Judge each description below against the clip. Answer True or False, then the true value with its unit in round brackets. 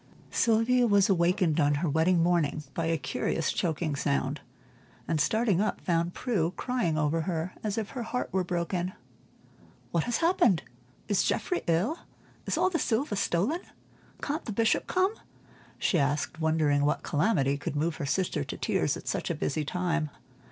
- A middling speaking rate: True (165 wpm)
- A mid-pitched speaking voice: True (175 Hz)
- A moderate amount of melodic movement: False (5.8 semitones)